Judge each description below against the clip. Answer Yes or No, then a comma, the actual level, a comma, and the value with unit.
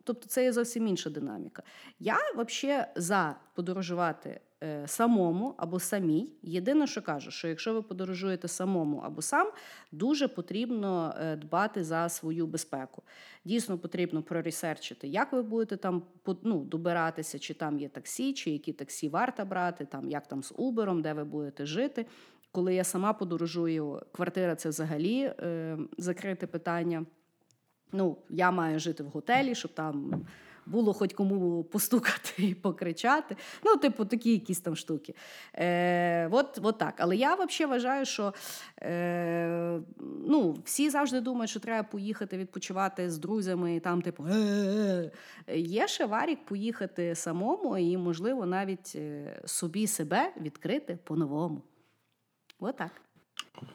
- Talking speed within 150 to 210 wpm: No, average, 135 wpm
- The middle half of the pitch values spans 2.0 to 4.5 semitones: No, average, 5.2 semitones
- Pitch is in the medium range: Yes, medium, 180 Hz